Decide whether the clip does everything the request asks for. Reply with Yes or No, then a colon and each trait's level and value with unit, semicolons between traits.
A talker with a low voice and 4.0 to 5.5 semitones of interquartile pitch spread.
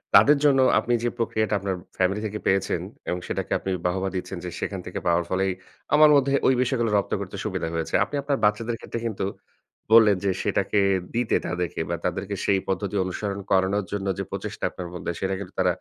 No: low, 100 Hz; average, 3.6 semitones